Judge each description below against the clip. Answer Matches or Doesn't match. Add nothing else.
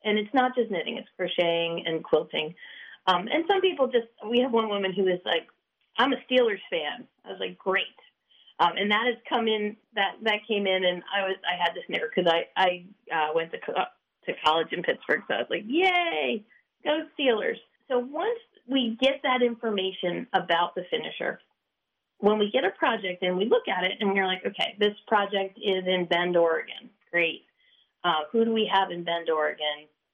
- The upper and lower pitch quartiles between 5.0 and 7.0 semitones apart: Matches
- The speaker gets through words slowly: Doesn't match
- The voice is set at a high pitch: Matches